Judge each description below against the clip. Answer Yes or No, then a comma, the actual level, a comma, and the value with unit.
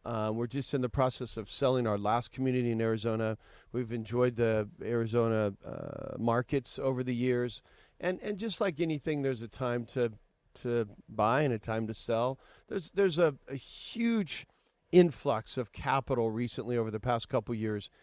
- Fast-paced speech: No, average, 185 wpm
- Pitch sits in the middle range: No, low, 120 Hz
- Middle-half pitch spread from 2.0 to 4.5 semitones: Yes, average, 3.2 semitones